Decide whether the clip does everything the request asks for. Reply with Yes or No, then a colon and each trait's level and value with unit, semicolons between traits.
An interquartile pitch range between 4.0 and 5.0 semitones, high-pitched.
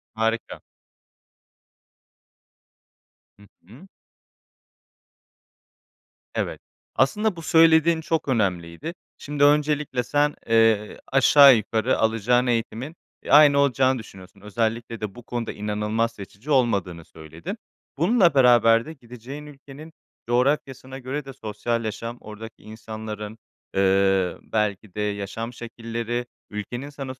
No: average, 4.6 semitones; low, 115 Hz